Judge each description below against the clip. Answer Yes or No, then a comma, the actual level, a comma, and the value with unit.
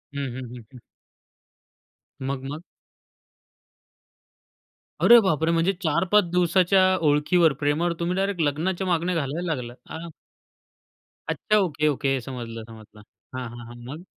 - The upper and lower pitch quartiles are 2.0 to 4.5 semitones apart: No, average, 5.1 semitones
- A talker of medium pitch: Yes, medium, 155 Hz